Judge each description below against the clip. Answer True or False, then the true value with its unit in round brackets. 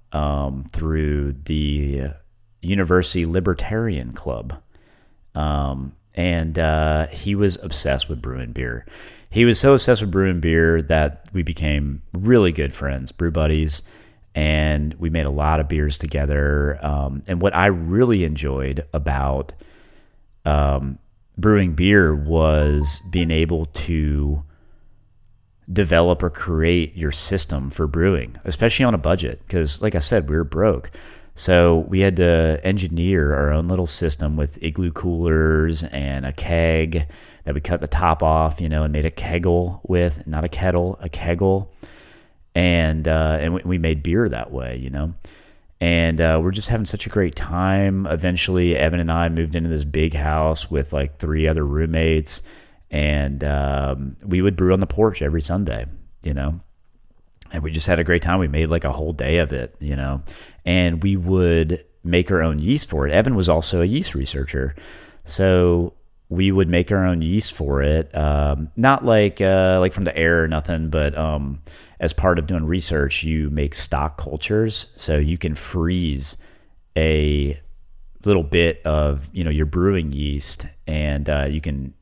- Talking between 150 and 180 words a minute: True (165 wpm)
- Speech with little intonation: False (3.3 semitones)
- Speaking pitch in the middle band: False (80 Hz)